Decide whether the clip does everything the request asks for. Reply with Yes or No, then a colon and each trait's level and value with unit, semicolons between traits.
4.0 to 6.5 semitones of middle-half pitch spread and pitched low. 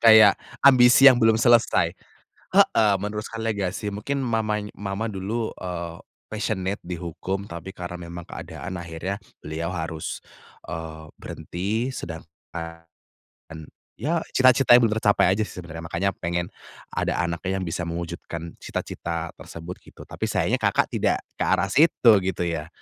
Yes: average, 4.5 semitones; very low, 95 Hz